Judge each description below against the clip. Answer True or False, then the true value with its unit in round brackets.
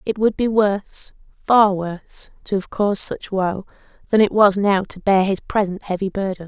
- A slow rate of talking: False (195 wpm)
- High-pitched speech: True (200 Hz)